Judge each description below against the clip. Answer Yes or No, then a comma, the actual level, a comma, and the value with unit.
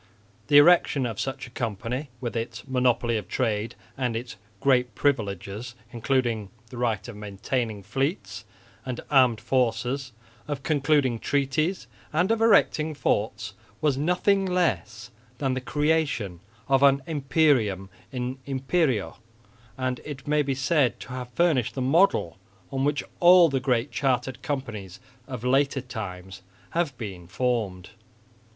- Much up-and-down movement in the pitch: No, average, 4.0 semitones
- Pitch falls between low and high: No, low, 130 Hz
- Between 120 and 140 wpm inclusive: Yes, slow, 135 wpm